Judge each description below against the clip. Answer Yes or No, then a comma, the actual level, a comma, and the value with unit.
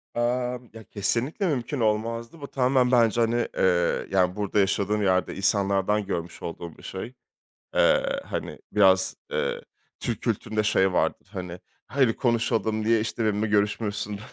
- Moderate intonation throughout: Yes, average, 3.4 semitones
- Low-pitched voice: Yes, low, 105 Hz